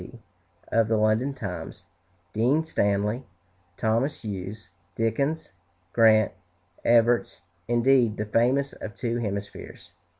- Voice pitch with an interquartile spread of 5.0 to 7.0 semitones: No, average, 2.8 semitones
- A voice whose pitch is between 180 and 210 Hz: No, low, 115 Hz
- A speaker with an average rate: No, slow, 105 wpm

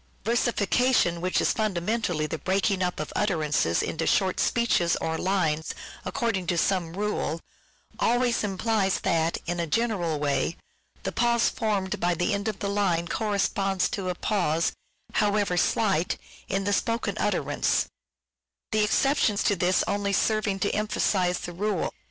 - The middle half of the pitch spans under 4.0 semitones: Yes, average, 3.5 semitones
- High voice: Yes, high, 195 Hz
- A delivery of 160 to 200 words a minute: No, average, 145 wpm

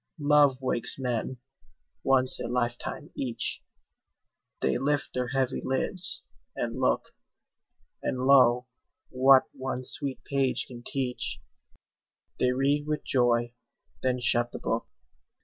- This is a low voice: Yes, low, 130 Hz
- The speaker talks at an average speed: No, slow, 115 wpm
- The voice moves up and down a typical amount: No, narrow, 1.8 semitones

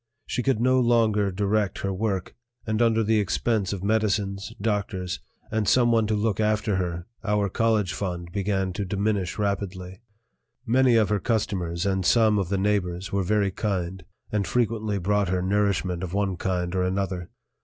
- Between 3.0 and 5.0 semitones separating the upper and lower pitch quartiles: No, narrow, 2.6 semitones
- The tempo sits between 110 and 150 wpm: No, average, 165 wpm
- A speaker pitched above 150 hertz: No, low, 100 Hz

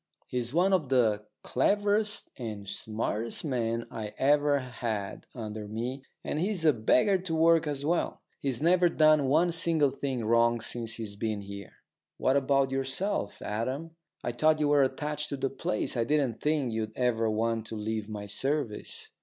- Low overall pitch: Yes, low, 130 Hz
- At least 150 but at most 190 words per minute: Yes, average, 170 wpm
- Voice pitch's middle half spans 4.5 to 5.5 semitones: Yes, average, 5.2 semitones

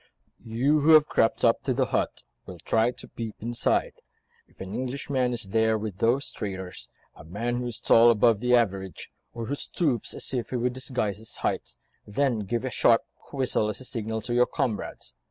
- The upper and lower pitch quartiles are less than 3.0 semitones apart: Yes, narrow, 2.5 semitones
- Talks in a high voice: No, low, 115 Hz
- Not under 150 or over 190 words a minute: No, average, 200 wpm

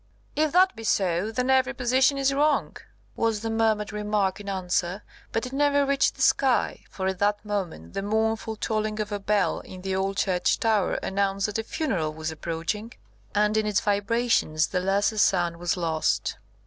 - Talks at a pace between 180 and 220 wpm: Yes, average, 185 wpm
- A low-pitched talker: No, high, 210 Hz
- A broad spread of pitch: No, average, 3.2 semitones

